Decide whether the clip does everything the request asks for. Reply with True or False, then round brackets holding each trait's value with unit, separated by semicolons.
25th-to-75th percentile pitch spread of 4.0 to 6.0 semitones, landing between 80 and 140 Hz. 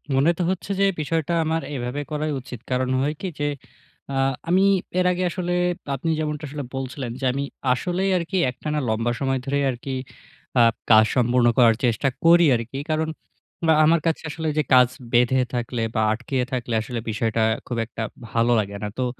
True (4.7 semitones; 135 Hz)